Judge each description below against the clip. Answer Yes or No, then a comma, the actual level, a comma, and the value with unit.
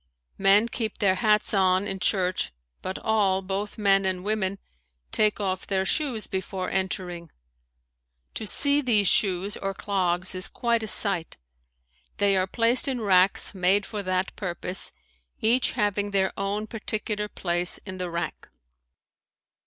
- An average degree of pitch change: No, narrow, 2.2 semitones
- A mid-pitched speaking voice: No, high, 195 Hz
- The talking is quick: No, average, 145 wpm